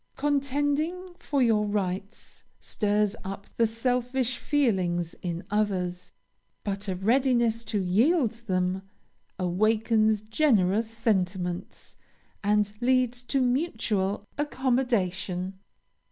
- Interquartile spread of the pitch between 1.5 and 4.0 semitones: No, average, 4.7 semitones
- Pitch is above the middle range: Yes, high, 215 Hz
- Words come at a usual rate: No, slow, 95 wpm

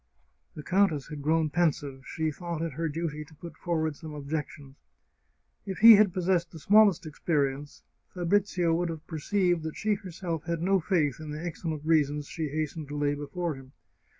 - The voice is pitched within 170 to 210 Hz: No, medium, 160 Hz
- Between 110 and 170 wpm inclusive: No, average, 180 wpm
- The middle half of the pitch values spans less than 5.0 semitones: Yes, average, 2.9 semitones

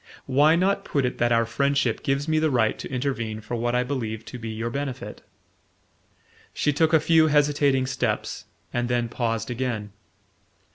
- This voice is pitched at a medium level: No, low, 130 Hz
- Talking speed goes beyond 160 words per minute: Yes, average, 175 wpm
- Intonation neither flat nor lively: Yes, average, 3.6 semitones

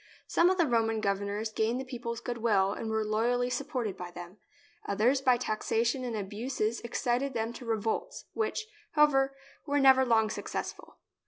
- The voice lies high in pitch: Yes, high, 235 Hz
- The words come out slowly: No, average, 165 wpm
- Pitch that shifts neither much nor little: Yes, average, 3.3 semitones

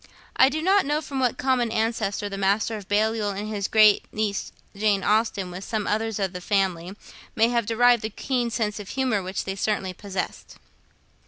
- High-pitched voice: Yes, high, 215 Hz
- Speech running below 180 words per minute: No, average, 190 wpm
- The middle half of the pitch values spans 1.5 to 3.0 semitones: Yes, average, 2.7 semitones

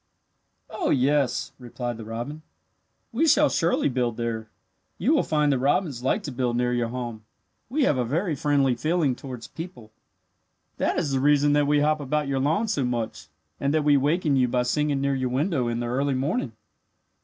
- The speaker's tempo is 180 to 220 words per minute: Yes, average, 190 wpm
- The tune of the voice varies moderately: Yes, average, 3.6 semitones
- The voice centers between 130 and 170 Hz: Yes, medium, 140 Hz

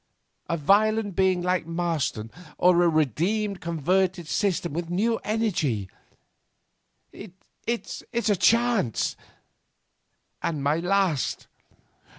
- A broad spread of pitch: No, average, 3.9 semitones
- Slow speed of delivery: Yes, slow, 95 wpm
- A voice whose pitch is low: No, medium, 180 Hz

